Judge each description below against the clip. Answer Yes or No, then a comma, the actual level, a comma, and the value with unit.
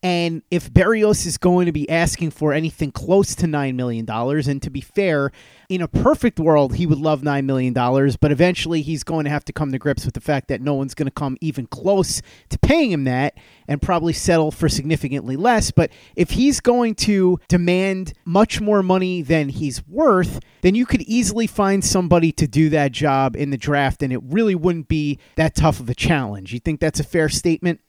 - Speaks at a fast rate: Yes, fast, 215 wpm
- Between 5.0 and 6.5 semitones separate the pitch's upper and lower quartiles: No, average, 4.2 semitones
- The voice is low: No, medium, 155 Hz